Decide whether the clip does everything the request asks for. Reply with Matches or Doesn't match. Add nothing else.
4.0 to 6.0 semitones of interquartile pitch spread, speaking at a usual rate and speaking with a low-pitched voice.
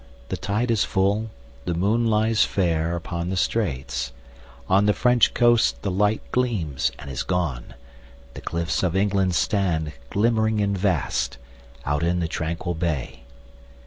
Doesn't match